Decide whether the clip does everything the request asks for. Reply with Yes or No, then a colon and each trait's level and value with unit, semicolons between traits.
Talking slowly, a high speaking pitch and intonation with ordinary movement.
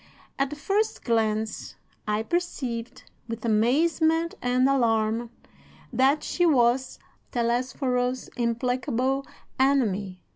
Yes: slow, 95 wpm; very high, 250 Hz; average, 3.1 semitones